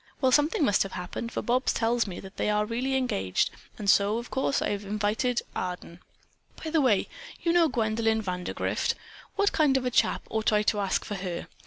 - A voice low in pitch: No, high, 220 Hz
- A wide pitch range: No, average, 4.4 semitones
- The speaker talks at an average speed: No, fast, 210 wpm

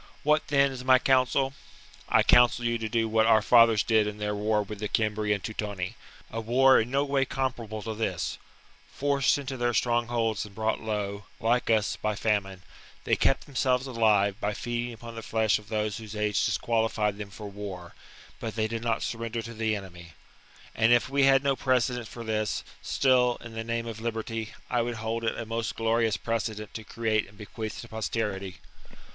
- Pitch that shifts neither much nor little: No, narrow, 2.2 semitones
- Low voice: Yes, low, 115 Hz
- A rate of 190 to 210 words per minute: Yes, average, 200 wpm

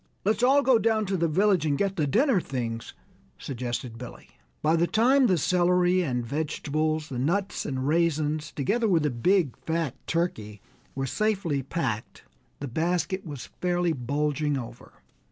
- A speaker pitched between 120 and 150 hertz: No, medium, 160 Hz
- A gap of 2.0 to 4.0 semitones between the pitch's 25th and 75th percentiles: No, average, 5.2 semitones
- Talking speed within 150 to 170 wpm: Yes, average, 155 wpm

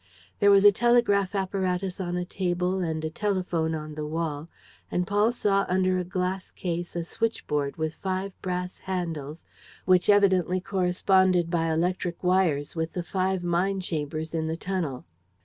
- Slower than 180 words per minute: Yes, average, 165 wpm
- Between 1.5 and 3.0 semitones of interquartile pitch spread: Yes, narrow, 2.6 semitones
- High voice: No, medium, 180 Hz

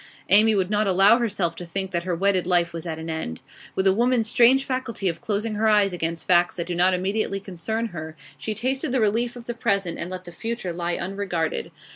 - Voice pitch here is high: Yes, high, 195 Hz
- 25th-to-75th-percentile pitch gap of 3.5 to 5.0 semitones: Yes, average, 4.2 semitones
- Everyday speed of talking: No, fast, 225 wpm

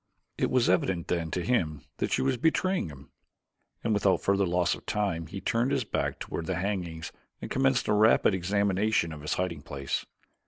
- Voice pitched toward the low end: Yes, very low, 95 Hz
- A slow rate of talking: No, average, 190 wpm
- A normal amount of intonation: Yes, average, 4.7 semitones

